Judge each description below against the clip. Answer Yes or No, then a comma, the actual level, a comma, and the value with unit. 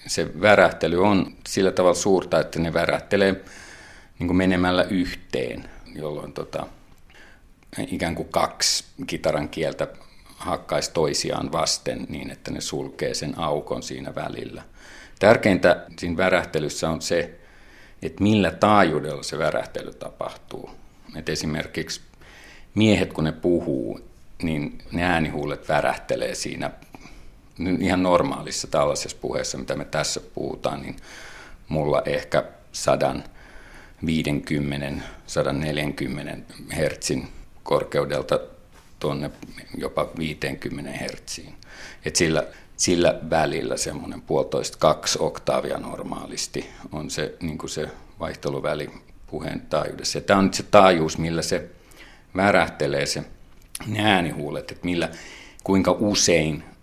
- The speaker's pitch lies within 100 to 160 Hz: No, very low, 90 Hz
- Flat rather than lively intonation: No, average, 3.3 semitones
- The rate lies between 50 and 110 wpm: Yes, average, 105 wpm